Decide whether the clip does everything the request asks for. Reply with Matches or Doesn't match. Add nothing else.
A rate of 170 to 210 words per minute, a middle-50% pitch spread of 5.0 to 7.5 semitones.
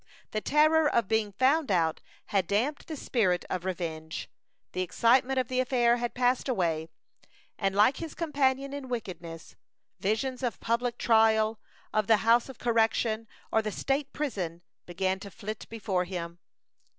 Doesn't match